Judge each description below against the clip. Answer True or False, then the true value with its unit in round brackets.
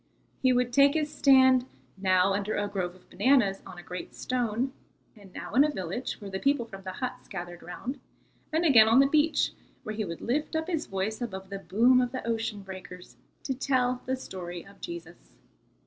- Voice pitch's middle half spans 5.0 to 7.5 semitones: True (5.4 semitones)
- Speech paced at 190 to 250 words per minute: True (200 wpm)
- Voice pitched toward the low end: False (220 Hz)